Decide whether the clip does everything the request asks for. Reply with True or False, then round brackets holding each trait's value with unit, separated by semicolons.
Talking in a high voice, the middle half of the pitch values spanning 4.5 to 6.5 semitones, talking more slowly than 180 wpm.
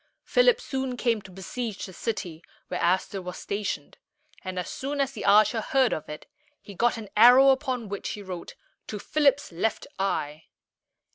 True (215 Hz; 5.6 semitones; 170 wpm)